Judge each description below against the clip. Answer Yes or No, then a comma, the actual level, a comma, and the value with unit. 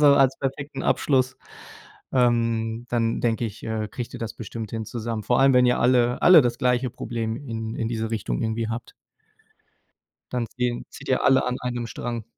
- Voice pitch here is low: Yes, low, 120 Hz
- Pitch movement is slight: Yes, narrow, 2.0 semitones